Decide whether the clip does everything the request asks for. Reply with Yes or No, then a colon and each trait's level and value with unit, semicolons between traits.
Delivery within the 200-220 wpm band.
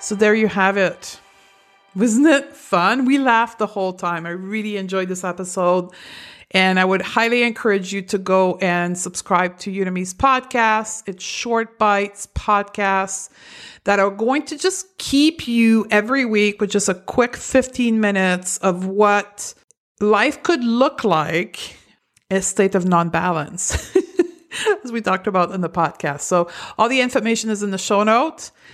No: average, 160 wpm